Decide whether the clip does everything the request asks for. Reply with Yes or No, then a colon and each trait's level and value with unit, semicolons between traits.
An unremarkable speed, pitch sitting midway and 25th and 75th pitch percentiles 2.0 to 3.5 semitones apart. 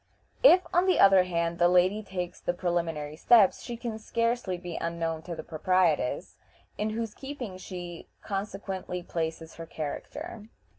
No: average, 150 wpm; medium, 180 Hz; average, 4.2 semitones